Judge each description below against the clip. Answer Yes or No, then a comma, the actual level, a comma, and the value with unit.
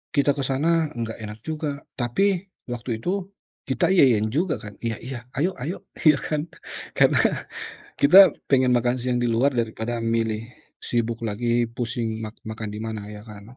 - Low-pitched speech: Yes, low, 120 Hz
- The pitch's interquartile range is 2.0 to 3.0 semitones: No, average, 4.1 semitones